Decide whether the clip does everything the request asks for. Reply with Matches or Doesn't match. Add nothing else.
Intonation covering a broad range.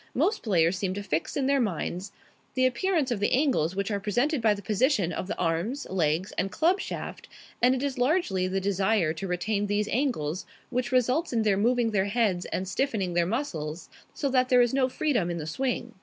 Matches